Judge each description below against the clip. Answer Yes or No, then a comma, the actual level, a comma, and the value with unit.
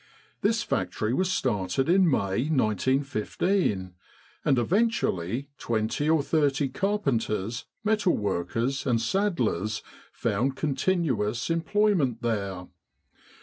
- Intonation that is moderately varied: No, wide, 7.7 semitones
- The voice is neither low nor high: No, low, 130 Hz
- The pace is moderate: No, slow, 95 wpm